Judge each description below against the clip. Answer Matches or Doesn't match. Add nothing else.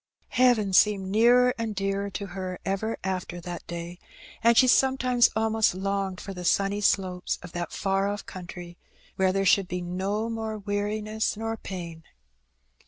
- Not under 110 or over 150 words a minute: Doesn't match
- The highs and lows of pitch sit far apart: Doesn't match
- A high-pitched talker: Matches